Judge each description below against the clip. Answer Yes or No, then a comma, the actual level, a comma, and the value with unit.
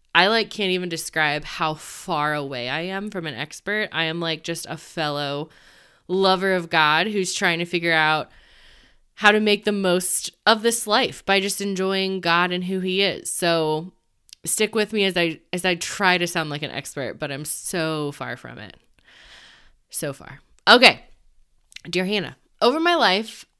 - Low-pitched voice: No, medium, 175 Hz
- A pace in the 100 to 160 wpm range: No, average, 180 wpm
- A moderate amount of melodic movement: Yes, average, 3.8 semitones